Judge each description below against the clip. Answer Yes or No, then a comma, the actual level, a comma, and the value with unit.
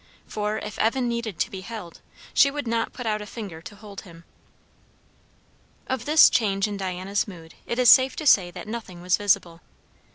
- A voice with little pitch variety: No, average, 4.0 semitones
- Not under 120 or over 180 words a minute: No, average, 190 wpm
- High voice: Yes, high, 210 Hz